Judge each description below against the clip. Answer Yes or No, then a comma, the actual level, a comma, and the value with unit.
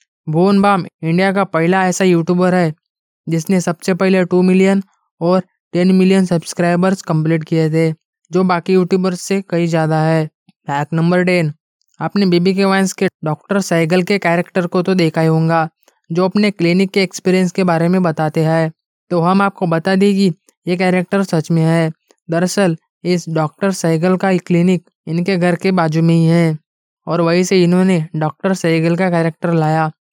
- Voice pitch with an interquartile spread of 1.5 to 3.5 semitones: Yes, narrow, 2.4 semitones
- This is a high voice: No, medium, 175 Hz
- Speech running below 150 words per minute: No, average, 175 wpm